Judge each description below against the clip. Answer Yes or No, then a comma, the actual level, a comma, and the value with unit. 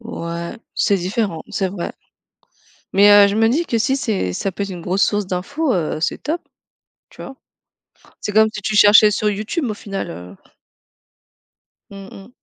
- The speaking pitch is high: Yes, high, 205 Hz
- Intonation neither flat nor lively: Yes, average, 3.2 semitones